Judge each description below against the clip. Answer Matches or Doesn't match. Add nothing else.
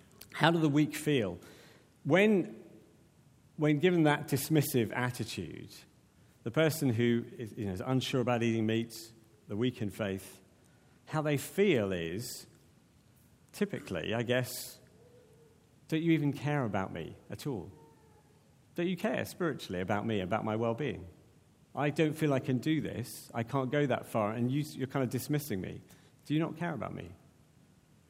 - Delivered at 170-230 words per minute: Doesn't match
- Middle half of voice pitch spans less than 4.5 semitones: Doesn't match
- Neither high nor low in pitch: Doesn't match